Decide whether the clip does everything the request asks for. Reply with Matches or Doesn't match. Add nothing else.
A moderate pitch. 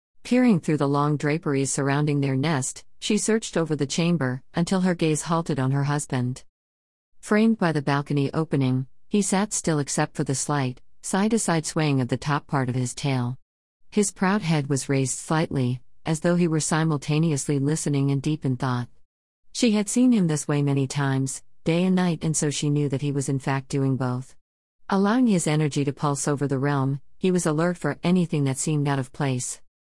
Matches